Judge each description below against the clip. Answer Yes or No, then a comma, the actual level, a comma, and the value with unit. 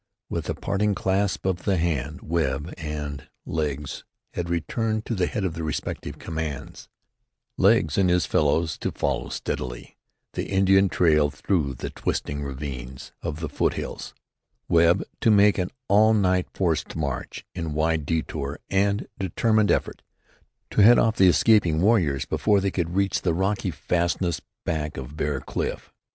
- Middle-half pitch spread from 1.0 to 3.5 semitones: No, average, 4.6 semitones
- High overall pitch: No, very low, 85 Hz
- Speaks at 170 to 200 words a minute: No, average, 155 wpm